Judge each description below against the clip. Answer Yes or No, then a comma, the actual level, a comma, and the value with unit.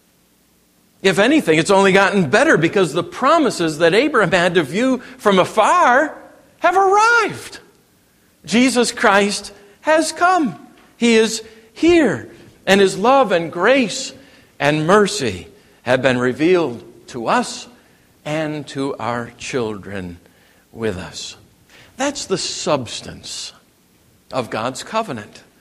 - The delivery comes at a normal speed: No, slow, 115 wpm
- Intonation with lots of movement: Yes, wide, 7.9 semitones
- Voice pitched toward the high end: Yes, high, 195 Hz